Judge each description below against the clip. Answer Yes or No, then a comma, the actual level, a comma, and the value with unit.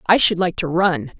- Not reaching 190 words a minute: No, fast, 250 wpm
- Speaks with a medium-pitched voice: Yes, medium, 180 Hz